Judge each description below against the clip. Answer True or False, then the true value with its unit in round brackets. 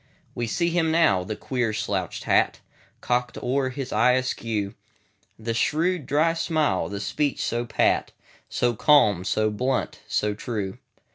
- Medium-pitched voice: False (120 Hz)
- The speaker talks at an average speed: False (125 wpm)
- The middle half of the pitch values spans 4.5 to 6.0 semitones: True (5.5 semitones)